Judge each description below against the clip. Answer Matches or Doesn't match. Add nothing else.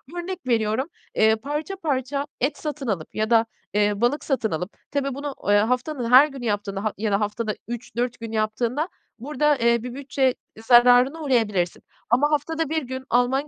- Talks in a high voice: Matches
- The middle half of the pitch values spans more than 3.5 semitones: Matches